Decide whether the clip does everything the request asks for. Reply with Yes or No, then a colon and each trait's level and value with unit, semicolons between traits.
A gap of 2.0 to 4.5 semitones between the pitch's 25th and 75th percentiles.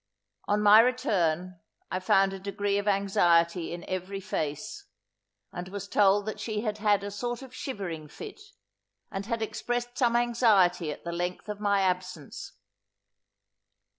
Yes: average, 3.2 semitones